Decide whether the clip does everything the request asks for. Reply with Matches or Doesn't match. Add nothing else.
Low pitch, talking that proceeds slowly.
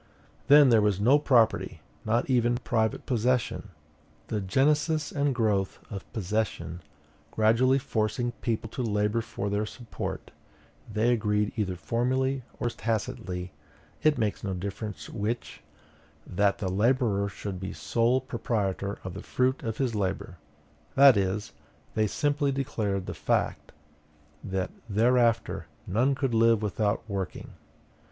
Matches